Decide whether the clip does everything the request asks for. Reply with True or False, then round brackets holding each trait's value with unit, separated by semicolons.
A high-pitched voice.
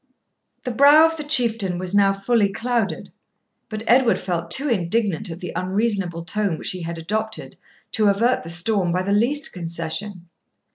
True (200 Hz)